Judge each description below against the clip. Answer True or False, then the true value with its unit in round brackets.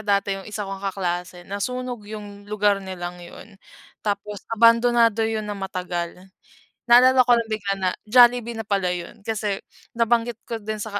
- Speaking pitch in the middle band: False (210 Hz)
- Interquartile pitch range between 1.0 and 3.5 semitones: True (2.9 semitones)